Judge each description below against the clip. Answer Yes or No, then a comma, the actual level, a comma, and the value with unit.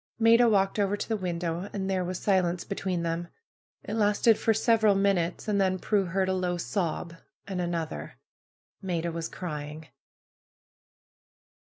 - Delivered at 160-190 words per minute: No, average, 150 wpm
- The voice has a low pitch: No, medium, 185 Hz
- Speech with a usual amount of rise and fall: Yes, average, 3.0 semitones